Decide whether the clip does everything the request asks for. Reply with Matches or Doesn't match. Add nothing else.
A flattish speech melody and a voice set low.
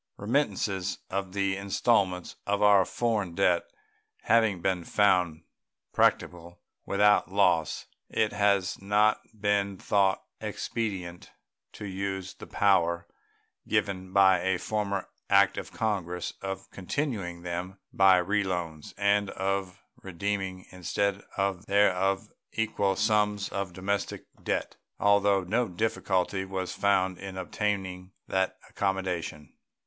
Matches